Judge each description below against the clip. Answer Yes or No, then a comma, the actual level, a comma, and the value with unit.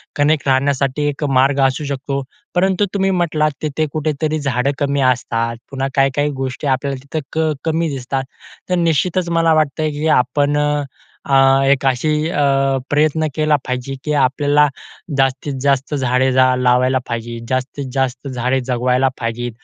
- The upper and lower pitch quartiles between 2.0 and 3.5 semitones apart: Yes, average, 2.8 semitones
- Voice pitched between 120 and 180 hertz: Yes, medium, 140 Hz